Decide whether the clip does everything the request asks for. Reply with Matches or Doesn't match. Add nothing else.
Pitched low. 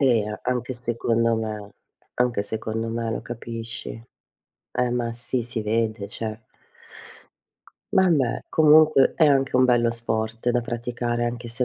Matches